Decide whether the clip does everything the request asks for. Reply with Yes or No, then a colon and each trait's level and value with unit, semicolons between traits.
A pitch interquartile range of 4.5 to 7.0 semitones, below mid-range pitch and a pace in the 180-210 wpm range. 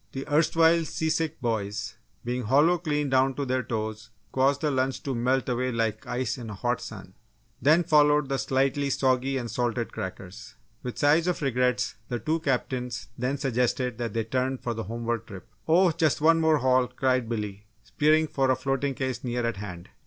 No: average, 3.6 semitones; low, 130 Hz; average, 185 wpm